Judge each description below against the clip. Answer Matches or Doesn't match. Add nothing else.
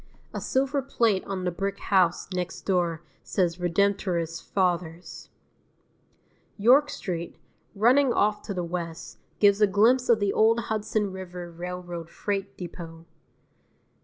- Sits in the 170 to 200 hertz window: Matches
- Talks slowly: Matches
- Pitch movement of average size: Matches